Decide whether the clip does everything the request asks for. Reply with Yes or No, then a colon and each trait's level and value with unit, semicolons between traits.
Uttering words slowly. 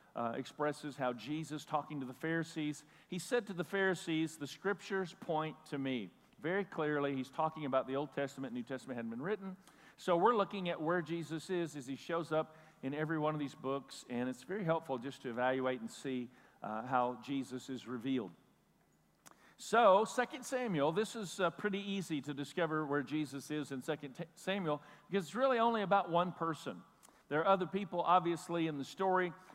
No: average, 190 wpm